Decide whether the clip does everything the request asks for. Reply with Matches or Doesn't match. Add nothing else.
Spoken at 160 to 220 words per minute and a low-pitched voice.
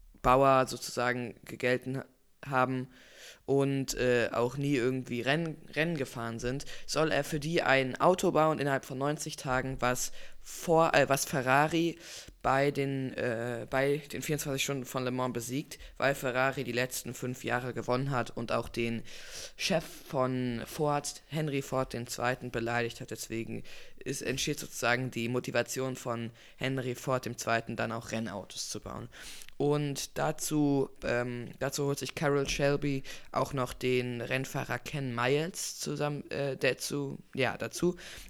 Doesn't match